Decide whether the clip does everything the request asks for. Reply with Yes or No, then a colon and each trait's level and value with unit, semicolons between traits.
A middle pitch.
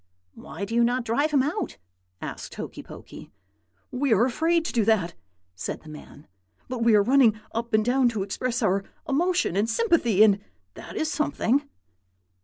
No: high, 235 Hz